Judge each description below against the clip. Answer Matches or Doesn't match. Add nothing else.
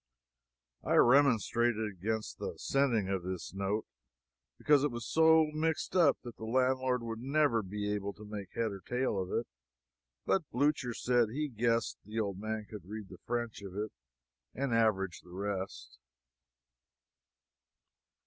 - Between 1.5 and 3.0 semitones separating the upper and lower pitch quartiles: Doesn't match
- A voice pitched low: Matches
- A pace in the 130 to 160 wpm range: Matches